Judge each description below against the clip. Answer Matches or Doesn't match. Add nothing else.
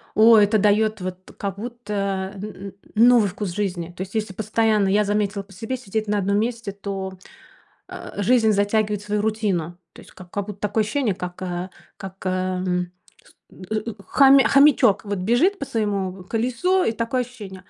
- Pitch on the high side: Matches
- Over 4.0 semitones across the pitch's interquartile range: Doesn't match